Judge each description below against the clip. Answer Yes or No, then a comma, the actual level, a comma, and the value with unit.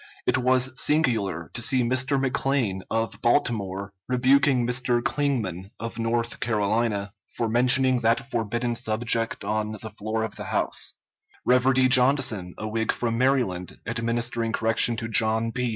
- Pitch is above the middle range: No, low, 115 Hz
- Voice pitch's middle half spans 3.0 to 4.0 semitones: No, narrow, 2.6 semitones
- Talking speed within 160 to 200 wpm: No, average, 140 wpm